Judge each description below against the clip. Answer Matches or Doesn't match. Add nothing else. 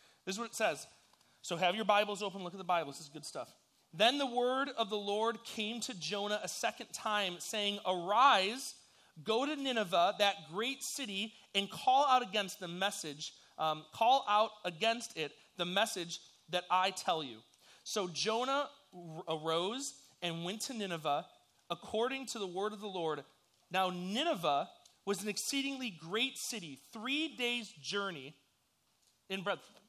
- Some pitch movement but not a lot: Matches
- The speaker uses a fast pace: Doesn't match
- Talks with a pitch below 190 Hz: Doesn't match